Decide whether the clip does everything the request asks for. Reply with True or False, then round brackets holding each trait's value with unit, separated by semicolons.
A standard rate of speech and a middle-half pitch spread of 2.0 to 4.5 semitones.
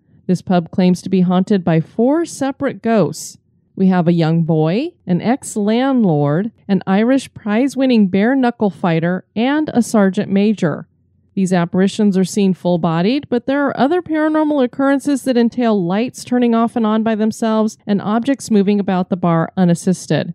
False (170 wpm; 5.0 semitones)